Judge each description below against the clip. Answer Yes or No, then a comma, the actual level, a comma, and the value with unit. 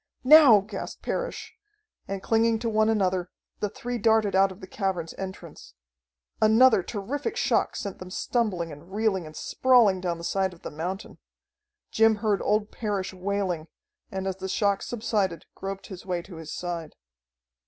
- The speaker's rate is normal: Yes, average, 165 wpm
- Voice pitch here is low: No, high, 195 Hz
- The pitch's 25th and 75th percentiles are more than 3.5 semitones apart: No, average, 3.2 semitones